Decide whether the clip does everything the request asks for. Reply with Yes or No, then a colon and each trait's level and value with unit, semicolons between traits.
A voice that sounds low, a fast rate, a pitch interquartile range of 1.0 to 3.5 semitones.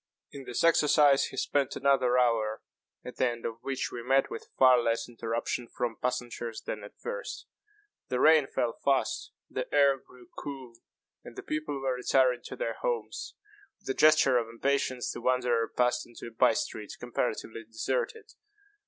No: low, 125 Hz; average, 170 wpm; average, 2.9 semitones